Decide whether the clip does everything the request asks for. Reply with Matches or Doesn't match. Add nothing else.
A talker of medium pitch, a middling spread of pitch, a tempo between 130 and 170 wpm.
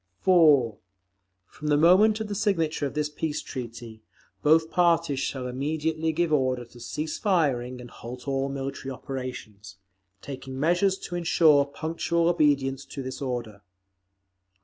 Matches